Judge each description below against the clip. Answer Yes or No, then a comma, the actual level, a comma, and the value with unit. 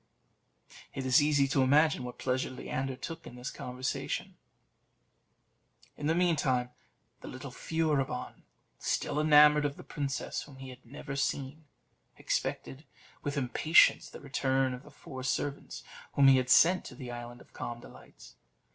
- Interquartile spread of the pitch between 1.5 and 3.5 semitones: Yes, narrow, 2.5 semitones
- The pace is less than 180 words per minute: Yes, average, 150 wpm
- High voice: No, low, 135 Hz